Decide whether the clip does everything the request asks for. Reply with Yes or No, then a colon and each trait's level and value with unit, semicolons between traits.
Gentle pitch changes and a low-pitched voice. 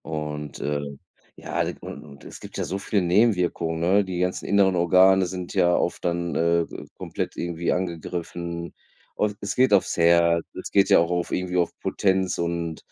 Yes: narrow, 1.8 semitones; very low, 85 Hz